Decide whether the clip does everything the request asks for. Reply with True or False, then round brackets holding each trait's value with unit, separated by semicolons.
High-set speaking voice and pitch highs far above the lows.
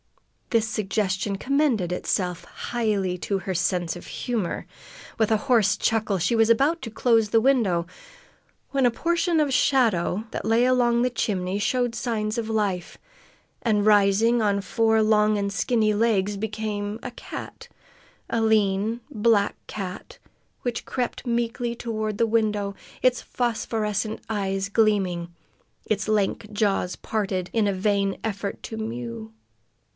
False (215 Hz; 2.7 semitones)